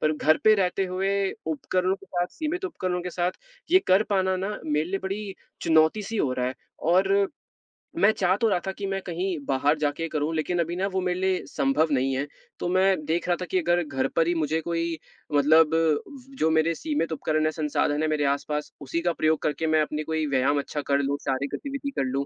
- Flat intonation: No, average, 3.9 semitones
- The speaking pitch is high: No, medium, 165 Hz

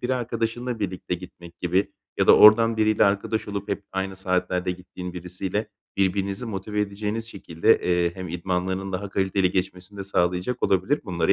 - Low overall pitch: Yes, very low, 95 Hz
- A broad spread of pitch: No, narrow, 2.5 semitones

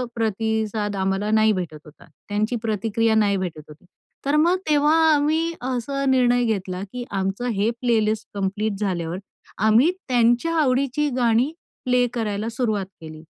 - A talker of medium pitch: No, high, 220 Hz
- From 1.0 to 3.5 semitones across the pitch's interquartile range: No, average, 3.9 semitones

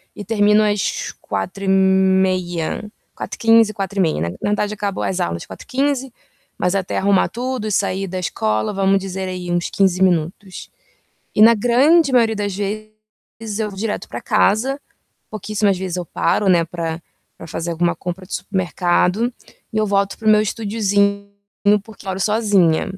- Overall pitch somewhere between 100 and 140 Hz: No, high, 200 Hz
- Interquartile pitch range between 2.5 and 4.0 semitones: Yes, average, 2.8 semitones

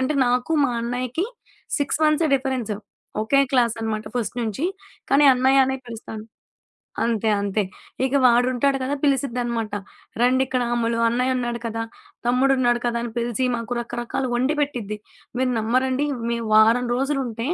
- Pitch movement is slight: Yes, narrow, 2.3 semitones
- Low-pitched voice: No, high, 245 Hz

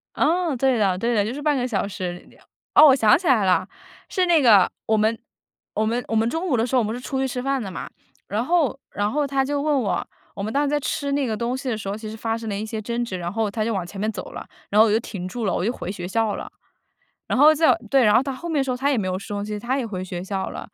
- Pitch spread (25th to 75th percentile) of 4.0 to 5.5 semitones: Yes, average, 4.7 semitones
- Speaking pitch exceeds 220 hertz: Yes, high, 230 Hz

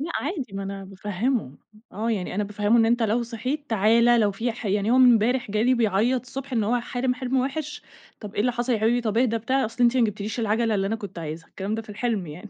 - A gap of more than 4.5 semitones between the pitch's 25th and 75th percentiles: No, average, 3.1 semitones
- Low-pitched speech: No, high, 225 Hz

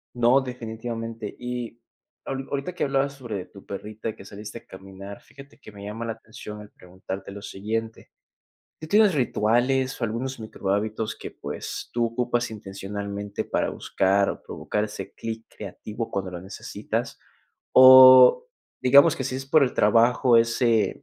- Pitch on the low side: Yes, low, 115 Hz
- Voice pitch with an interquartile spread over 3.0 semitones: Yes, average, 3.7 semitones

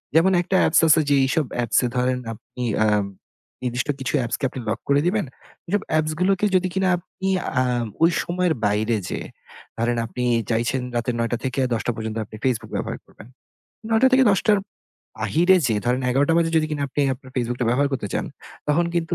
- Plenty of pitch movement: Yes, wide, 6.2 semitones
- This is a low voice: Yes, low, 130 Hz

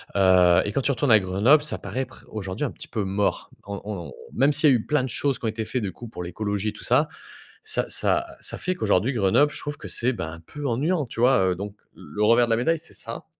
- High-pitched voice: No, low, 115 Hz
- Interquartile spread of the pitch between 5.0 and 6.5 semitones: Yes, wide, 5.6 semitones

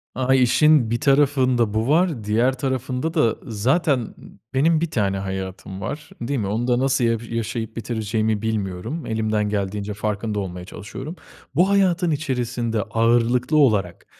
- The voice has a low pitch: Yes, low, 115 Hz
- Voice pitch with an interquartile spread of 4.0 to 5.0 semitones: Yes, average, 4.4 semitones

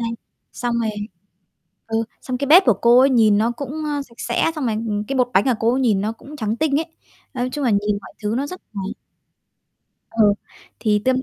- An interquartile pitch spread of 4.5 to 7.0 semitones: No, average, 4.0 semitones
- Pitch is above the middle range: Yes, high, 240 Hz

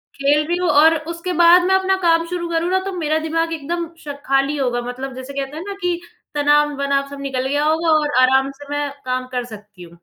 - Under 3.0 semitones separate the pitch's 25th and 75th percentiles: No, average, 3.6 semitones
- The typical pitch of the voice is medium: No, very high, 290 Hz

